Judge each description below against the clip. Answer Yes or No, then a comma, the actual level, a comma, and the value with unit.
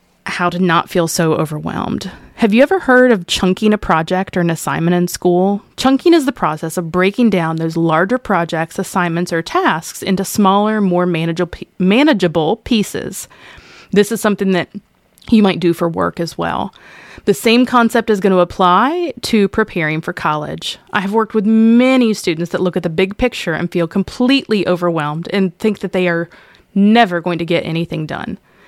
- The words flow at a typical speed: Yes, average, 180 wpm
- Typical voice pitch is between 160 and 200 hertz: Yes, medium, 185 Hz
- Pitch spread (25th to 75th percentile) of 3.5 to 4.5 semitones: Yes, average, 4.1 semitones